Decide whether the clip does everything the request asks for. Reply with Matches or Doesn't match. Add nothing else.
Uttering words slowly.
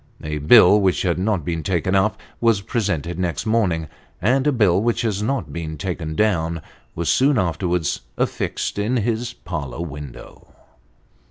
Doesn't match